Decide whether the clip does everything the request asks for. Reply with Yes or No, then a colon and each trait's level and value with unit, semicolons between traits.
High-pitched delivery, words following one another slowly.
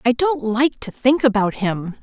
No: high, 240 Hz; fast, 205 wpm